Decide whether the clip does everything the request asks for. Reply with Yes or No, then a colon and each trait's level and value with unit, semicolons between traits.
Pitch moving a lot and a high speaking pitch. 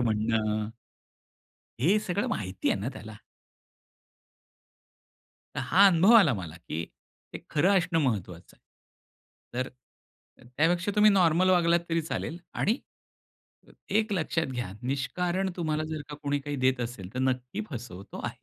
No: wide, 7.2 semitones; medium, 145 Hz